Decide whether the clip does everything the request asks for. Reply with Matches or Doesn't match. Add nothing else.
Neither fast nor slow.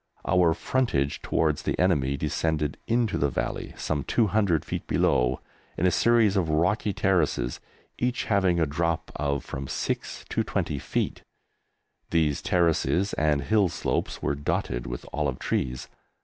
Matches